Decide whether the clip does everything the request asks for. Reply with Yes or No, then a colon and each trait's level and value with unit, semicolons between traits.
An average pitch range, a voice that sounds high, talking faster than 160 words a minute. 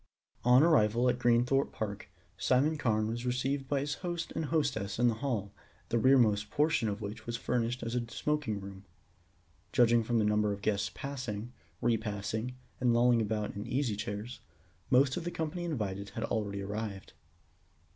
No: average, 3.8 semitones; low, 120 Hz; average, 175 wpm